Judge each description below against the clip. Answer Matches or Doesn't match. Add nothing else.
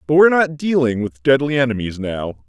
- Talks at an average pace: Matches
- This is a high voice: Doesn't match